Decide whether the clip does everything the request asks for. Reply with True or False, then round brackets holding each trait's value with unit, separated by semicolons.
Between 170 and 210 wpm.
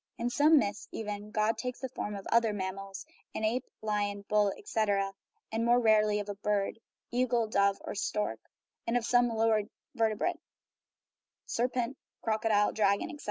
False (160 wpm)